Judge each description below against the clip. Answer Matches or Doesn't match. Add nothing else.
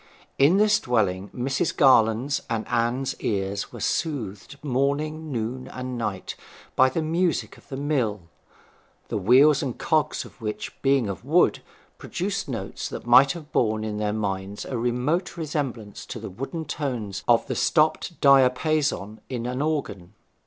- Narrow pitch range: Doesn't match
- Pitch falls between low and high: Doesn't match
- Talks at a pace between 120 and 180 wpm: Matches